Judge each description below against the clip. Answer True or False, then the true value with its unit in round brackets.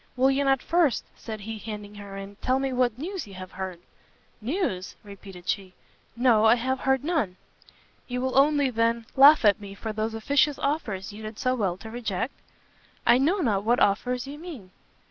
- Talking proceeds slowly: False (190 wpm)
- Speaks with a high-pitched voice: True (230 Hz)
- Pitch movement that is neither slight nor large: True (4.9 semitones)